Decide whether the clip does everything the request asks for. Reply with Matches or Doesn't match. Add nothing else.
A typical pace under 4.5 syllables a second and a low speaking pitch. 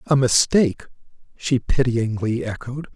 Matches